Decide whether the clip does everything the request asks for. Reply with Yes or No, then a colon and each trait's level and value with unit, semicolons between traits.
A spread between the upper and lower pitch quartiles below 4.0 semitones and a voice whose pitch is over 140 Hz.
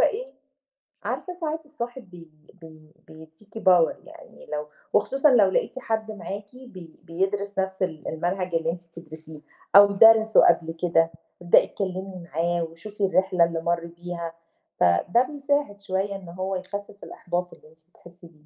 Yes: average, 3.5 semitones; medium, 185 Hz